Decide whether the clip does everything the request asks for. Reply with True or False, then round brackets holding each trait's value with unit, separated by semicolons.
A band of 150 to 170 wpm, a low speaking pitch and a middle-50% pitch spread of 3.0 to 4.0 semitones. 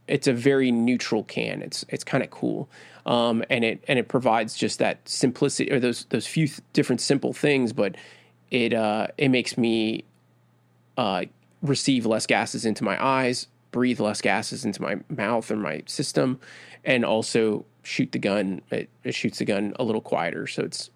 False (185 wpm; 120 Hz; 3.4 semitones)